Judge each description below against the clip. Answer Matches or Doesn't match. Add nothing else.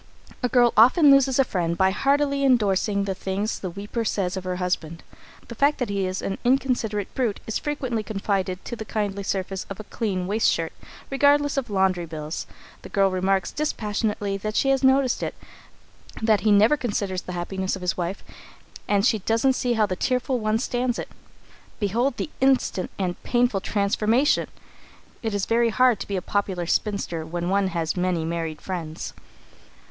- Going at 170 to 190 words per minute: Matches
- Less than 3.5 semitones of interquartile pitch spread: Doesn't match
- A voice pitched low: Doesn't match